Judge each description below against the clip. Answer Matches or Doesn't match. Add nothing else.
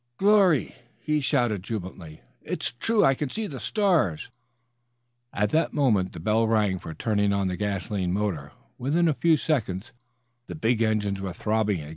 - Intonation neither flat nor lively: Doesn't match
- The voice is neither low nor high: Doesn't match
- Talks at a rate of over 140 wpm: Matches